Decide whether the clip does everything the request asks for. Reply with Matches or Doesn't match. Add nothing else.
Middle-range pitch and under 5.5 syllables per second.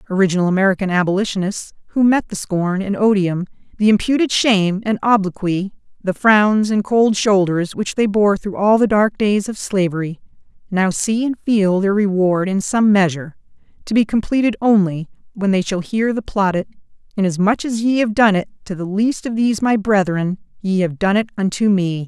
Doesn't match